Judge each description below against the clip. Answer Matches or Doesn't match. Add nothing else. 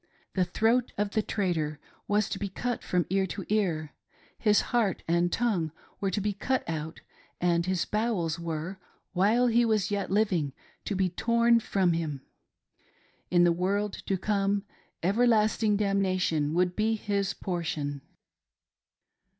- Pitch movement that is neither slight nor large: Matches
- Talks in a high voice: Matches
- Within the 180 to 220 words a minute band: Doesn't match